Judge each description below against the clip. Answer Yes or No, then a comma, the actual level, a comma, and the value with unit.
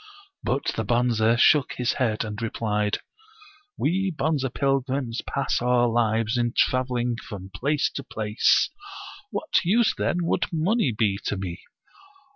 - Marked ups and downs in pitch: No, average, 4.0 semitones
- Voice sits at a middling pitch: No, low, 120 Hz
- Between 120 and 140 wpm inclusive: Yes, slow, 135 wpm